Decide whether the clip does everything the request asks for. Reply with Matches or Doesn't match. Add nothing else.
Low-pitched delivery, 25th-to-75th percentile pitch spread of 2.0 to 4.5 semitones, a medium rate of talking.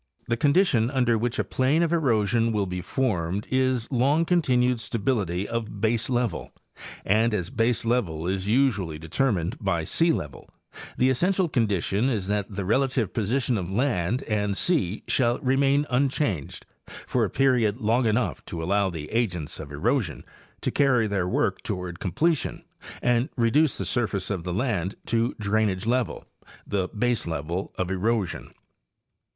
Doesn't match